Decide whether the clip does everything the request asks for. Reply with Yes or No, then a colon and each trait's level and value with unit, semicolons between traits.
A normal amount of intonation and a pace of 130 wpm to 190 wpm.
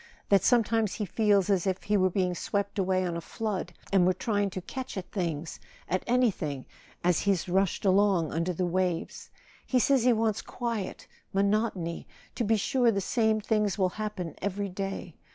Yes: average, 3.1 semitones; average, 170 wpm